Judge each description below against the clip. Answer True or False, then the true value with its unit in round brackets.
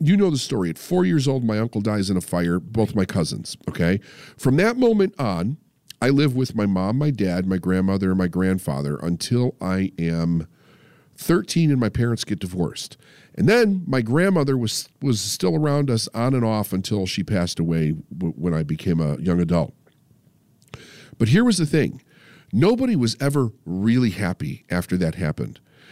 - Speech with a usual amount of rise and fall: False (7.9 semitones)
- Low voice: True (115 Hz)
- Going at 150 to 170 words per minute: False (180 wpm)